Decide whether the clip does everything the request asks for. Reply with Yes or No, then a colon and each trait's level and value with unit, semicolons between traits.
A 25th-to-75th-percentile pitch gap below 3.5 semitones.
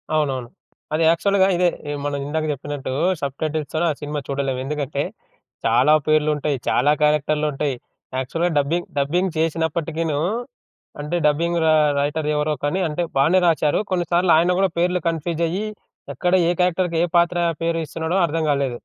Yes: average, 2.8 semitones